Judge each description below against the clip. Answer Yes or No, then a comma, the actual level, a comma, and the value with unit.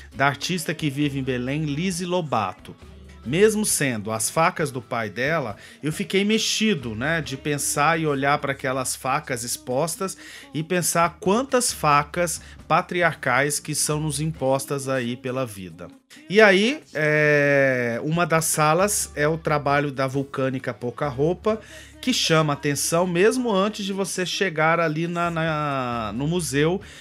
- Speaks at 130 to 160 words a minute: Yes, average, 145 wpm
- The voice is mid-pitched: Yes, medium, 150 Hz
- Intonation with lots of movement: No, average, 4.7 semitones